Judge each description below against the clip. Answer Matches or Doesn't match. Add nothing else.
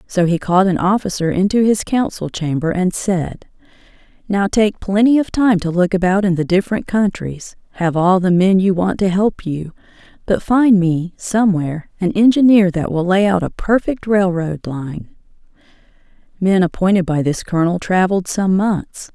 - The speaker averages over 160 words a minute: Matches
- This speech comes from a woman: Matches